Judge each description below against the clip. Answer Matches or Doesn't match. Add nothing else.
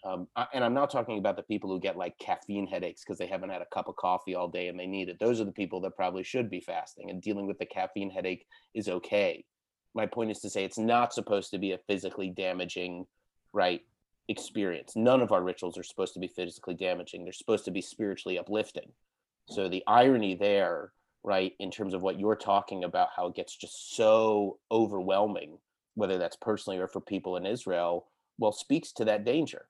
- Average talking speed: Doesn't match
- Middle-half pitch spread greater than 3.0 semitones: Doesn't match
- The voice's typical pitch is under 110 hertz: Matches